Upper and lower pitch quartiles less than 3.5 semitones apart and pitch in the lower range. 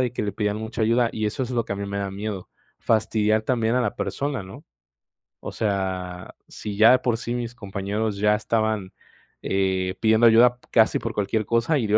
Yes: narrow, 2.6 semitones; low, 110 Hz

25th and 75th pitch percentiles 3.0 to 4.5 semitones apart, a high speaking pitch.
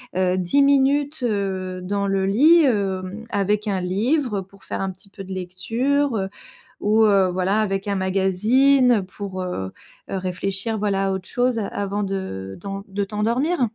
Yes: average, 3.3 semitones; high, 200 Hz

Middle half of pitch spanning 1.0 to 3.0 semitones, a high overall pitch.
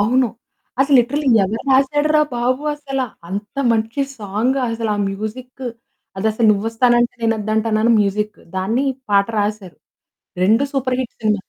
No: average, 3.5 semitones; high, 225 Hz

